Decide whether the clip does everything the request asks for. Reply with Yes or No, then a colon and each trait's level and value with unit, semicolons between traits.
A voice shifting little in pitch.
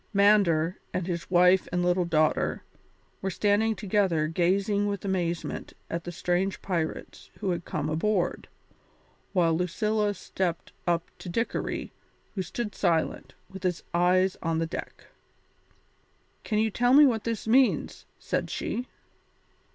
No: average, 3.3 semitones